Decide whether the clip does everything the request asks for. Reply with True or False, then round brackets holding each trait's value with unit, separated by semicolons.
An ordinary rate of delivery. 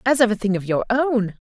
False (285 wpm)